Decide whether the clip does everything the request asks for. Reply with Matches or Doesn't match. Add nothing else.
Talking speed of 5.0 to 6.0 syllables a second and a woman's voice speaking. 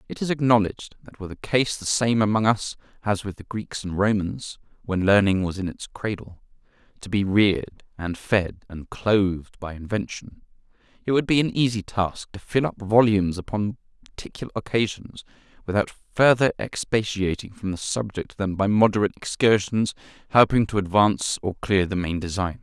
Doesn't match